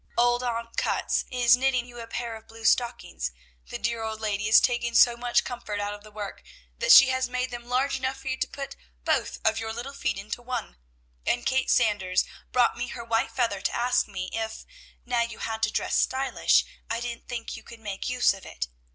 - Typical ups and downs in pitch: No, narrow, 2.0 semitones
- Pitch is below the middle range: No, high, 235 Hz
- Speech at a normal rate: No, fast, 220 wpm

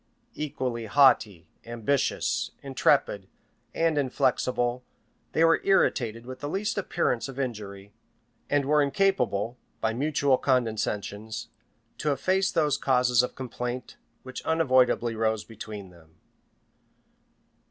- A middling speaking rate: No, slow, 110 wpm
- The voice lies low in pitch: Yes, low, 125 Hz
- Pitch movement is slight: No, average, 4.4 semitones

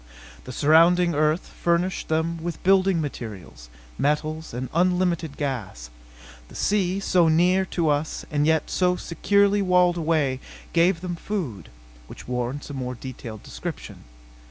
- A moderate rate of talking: No, slow, 130 wpm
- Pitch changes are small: No, average, 4.6 semitones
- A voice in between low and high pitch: Yes, medium, 160 Hz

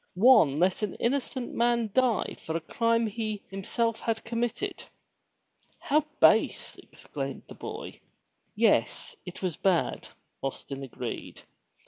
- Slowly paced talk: Yes, slow, 120 wpm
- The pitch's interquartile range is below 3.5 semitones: No, average, 4.5 semitones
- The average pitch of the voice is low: No, high, 225 Hz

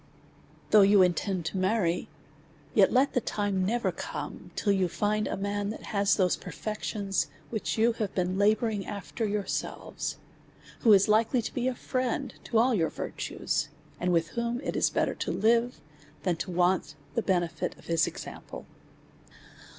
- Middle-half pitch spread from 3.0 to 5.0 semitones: Yes, average, 3.4 semitones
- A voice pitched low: No, high, 205 Hz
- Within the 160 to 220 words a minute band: Yes, average, 165 wpm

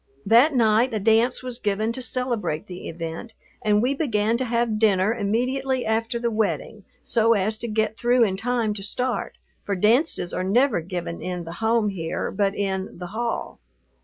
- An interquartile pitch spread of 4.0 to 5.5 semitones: No, average, 3.3 semitones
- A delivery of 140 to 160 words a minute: No, average, 180 wpm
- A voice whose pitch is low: No, high, 220 Hz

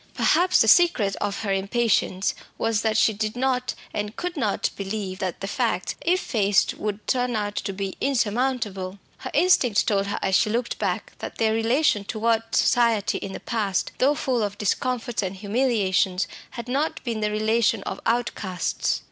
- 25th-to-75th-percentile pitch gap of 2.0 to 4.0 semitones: Yes, average, 3.5 semitones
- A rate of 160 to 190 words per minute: Yes, average, 175 wpm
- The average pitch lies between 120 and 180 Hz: No, high, 220 Hz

